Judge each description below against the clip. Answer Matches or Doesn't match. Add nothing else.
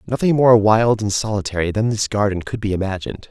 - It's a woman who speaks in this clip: Doesn't match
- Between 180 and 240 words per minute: Matches